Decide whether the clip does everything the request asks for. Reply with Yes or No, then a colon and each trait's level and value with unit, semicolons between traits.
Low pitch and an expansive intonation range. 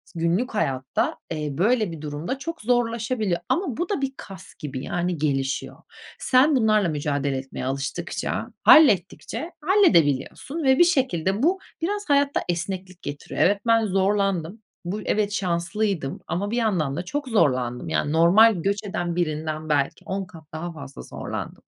No: medium, 185 Hz; wide, 6.8 semitones